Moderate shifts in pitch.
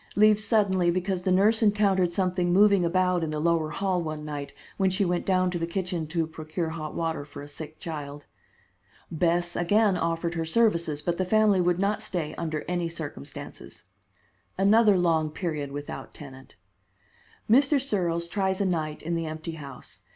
Yes: average, 3.3 semitones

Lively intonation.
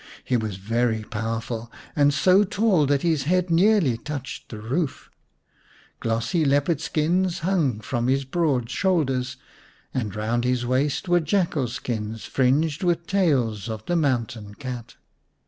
Yes: wide, 6.2 semitones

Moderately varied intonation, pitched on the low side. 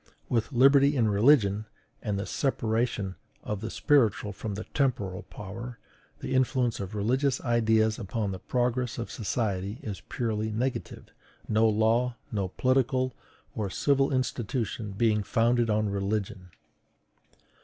Yes: average, 3.2 semitones; low, 110 Hz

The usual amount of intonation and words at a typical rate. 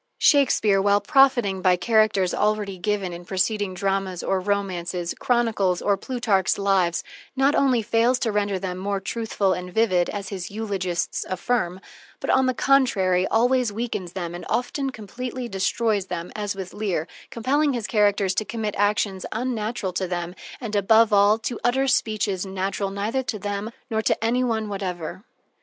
Yes: average, 3.4 semitones; average, 160 wpm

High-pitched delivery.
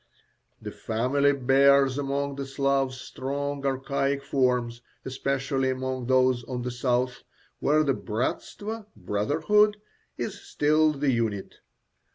No: low, 135 Hz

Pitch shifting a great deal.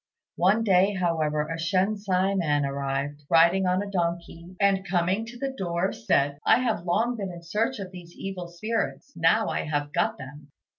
No: average, 3.4 semitones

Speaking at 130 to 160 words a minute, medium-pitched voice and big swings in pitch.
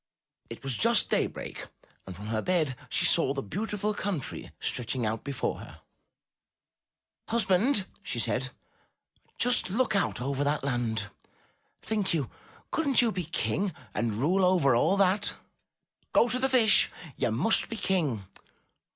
Yes: average, 140 wpm; medium, 175 Hz; wide, 8.5 semitones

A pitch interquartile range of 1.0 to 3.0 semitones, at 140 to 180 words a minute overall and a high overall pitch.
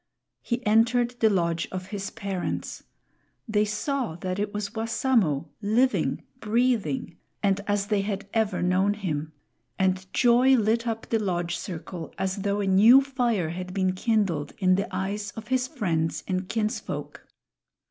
No: average, 3.5 semitones; average, 150 wpm; high, 205 Hz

